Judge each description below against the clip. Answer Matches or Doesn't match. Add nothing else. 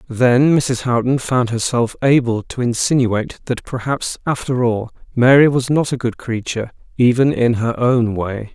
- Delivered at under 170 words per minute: Matches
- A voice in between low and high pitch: Doesn't match